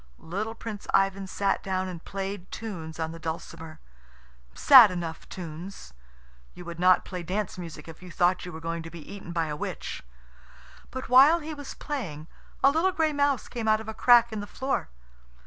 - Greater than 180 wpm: Yes, average, 190 wpm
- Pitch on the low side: No, high, 190 Hz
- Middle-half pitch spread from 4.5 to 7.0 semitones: Yes, wide, 5.4 semitones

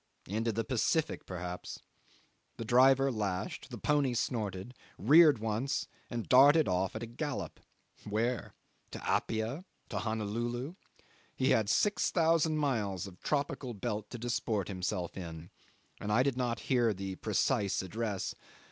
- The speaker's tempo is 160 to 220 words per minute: No, slow, 135 wpm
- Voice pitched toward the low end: Yes, low, 115 Hz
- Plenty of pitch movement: No, average, 4.5 semitones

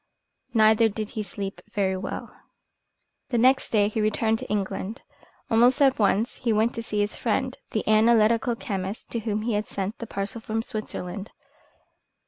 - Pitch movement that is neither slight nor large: No, narrow, 2.0 semitones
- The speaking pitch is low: No, high, 215 Hz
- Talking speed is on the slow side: No, average, 165 wpm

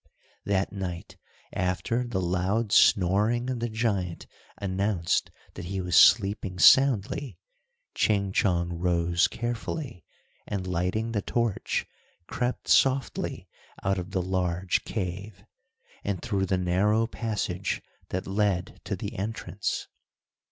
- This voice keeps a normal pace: No, slow, 115 wpm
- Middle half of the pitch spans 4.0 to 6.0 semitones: No, average, 3.5 semitones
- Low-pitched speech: Yes, very low, 95 Hz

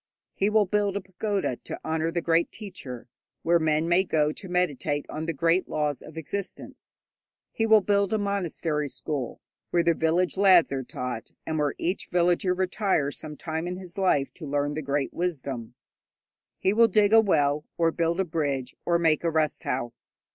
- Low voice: No, medium, 165 Hz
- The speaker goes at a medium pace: Yes, average, 190 wpm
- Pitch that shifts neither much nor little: Yes, average, 4.1 semitones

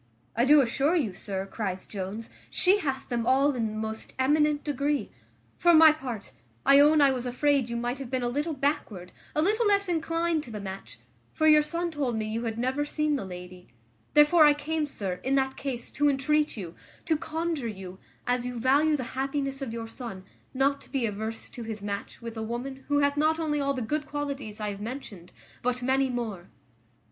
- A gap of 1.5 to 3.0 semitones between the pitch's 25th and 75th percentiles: No, average, 4.7 semitones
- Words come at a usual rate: No, fast, 210 wpm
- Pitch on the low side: No, very high, 265 Hz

